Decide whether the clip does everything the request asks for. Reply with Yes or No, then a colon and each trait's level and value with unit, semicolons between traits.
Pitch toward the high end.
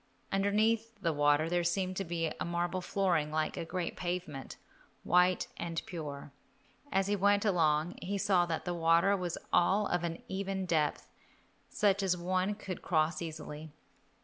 No: medium, 175 Hz